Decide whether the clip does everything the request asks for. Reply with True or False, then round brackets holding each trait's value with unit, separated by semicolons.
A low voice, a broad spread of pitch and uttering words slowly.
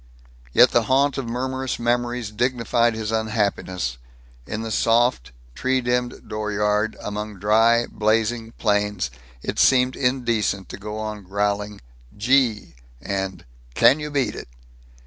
False (110 Hz; 2.9 semitones; 125 wpm)